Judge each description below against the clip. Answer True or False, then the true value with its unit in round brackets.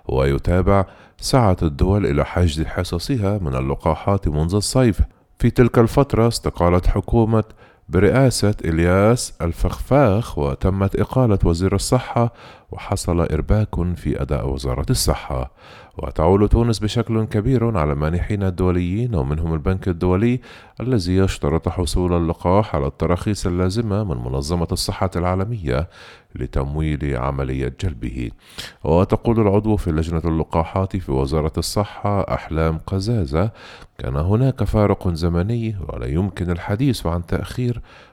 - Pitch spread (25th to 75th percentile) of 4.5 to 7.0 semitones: True (4.8 semitones)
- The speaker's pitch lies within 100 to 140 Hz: False (90 Hz)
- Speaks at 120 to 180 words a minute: False (110 wpm)